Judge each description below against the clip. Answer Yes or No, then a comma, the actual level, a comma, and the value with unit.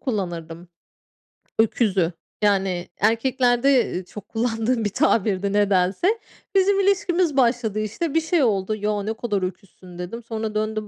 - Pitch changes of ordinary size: Yes, average, 4.5 semitones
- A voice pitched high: Yes, high, 215 Hz